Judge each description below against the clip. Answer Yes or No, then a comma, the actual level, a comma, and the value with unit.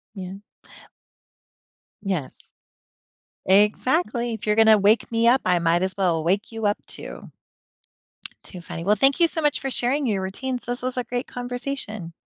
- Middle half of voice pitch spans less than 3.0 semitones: No, average, 4.7 semitones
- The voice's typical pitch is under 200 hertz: No, high, 220 Hz